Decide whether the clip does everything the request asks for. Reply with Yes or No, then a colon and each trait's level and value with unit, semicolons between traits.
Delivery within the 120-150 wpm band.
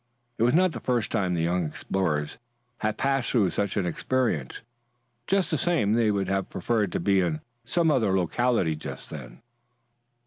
No: average, 175 wpm